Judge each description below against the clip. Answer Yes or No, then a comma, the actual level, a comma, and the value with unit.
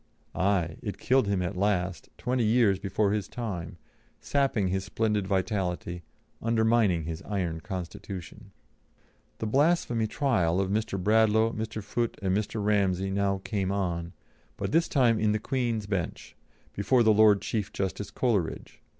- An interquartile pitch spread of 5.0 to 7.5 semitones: No, average, 3.0 semitones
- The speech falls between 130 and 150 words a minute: Yes, average, 145 wpm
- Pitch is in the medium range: No, low, 100 Hz